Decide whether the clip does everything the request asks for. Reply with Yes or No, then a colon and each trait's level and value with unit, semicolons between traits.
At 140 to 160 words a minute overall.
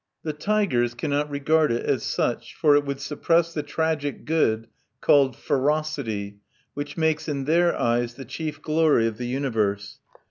Yes: average, 155 wpm